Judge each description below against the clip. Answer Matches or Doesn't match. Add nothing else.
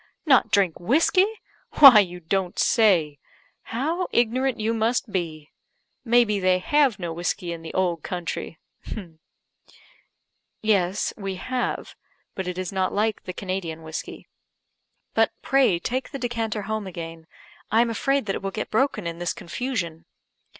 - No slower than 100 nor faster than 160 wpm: Matches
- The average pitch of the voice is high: Matches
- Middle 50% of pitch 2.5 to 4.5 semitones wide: Doesn't match